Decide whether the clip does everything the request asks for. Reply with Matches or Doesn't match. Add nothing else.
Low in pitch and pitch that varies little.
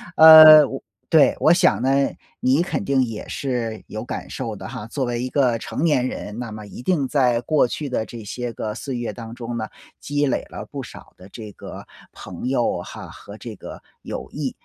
Doesn't match